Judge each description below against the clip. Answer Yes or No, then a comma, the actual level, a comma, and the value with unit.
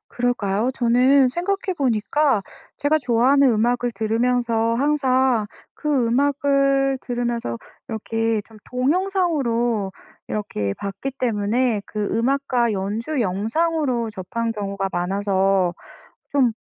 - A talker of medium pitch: No, high, 240 Hz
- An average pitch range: Yes, average, 4.3 semitones